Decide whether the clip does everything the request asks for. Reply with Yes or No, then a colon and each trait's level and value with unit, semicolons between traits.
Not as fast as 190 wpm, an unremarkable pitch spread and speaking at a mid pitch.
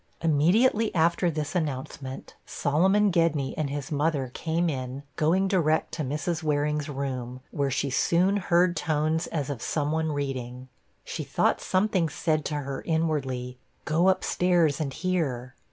Yes: average, 150 wpm; average, 3.6 semitones; medium, 155 Hz